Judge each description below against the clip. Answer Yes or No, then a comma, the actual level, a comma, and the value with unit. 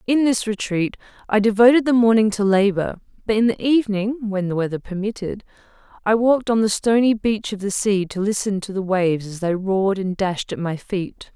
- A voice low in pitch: No, high, 205 Hz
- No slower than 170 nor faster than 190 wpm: No, fast, 205 wpm